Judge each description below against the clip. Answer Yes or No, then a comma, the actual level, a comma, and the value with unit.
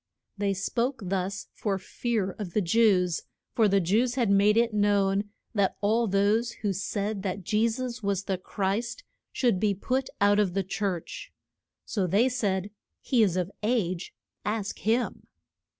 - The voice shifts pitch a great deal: No, average, 2.8 semitones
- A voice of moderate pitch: No, high, 205 Hz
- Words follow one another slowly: No, average, 160 wpm